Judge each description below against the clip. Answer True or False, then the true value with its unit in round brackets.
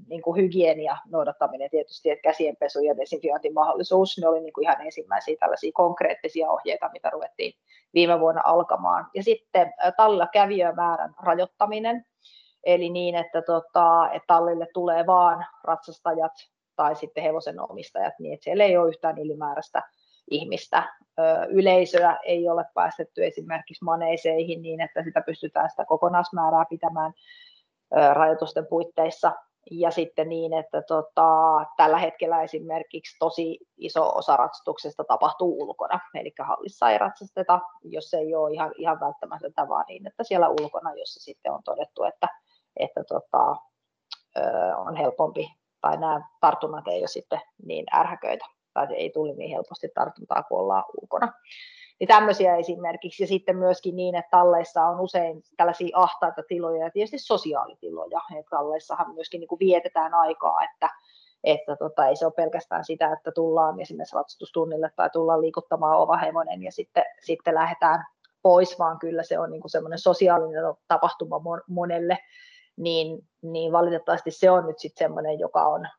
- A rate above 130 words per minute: True (145 wpm)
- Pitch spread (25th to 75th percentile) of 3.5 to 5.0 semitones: False (2.7 semitones)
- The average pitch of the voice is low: False (170 Hz)